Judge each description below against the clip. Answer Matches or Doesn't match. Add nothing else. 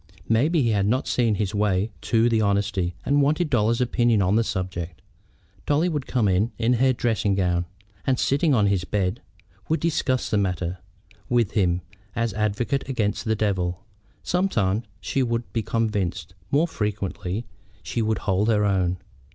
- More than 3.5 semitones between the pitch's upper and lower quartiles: Matches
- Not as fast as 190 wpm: Matches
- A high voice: Doesn't match